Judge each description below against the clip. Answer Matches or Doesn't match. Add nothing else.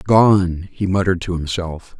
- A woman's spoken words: Doesn't match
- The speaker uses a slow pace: Doesn't match